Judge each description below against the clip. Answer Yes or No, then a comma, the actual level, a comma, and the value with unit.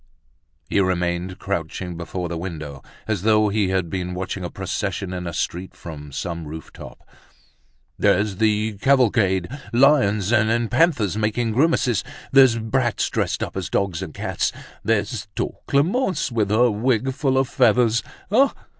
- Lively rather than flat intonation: No, average, 4.7 semitones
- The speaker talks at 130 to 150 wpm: Yes, average, 140 wpm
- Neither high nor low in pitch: No, low, 105 Hz